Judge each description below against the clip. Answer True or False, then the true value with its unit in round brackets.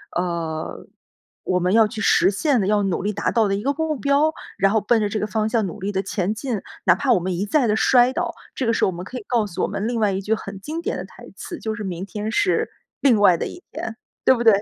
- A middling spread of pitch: True (4.0 semitones)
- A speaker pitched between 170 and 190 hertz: False (215 Hz)